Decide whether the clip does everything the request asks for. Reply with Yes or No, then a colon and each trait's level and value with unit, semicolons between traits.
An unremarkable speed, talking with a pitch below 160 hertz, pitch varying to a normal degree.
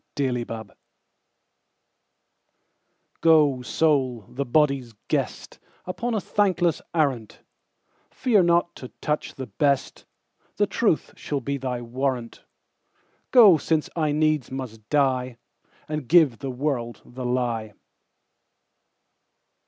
No: slow, 90 wpm; low, 135 Hz; average, 4.1 semitones